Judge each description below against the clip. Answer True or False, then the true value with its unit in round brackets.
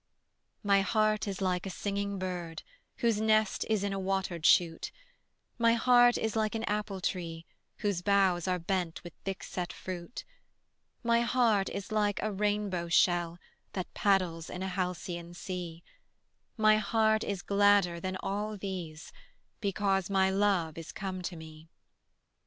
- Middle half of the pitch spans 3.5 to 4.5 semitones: False (3.0 semitones)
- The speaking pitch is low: False (195 Hz)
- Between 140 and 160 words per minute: True (150 wpm)